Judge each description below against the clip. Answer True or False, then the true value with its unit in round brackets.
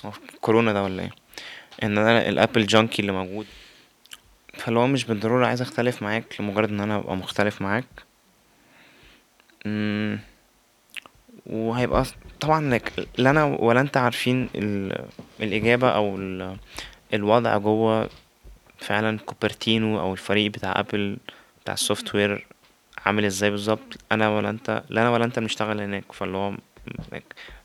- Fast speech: False (125 wpm)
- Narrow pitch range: True (2.1 semitones)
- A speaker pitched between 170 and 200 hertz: False (110 Hz)